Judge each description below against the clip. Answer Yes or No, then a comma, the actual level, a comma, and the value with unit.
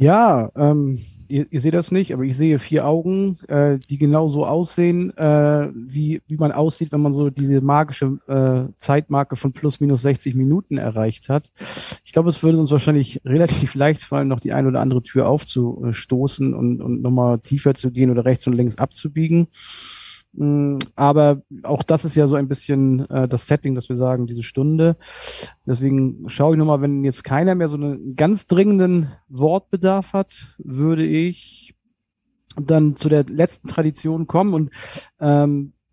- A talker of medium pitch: Yes, medium, 145 Hz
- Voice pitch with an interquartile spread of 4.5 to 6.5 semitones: No, average, 3.0 semitones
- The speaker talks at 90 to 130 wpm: No, average, 170 wpm